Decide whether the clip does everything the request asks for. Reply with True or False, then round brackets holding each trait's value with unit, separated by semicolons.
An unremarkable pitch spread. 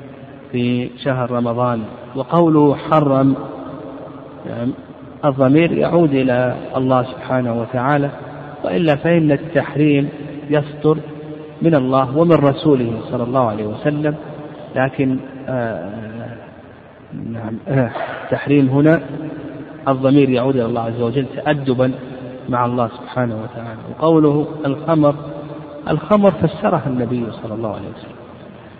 True (3.3 semitones)